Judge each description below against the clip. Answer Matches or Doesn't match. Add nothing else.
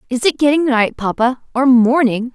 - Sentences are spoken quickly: Doesn't match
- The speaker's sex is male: Doesn't match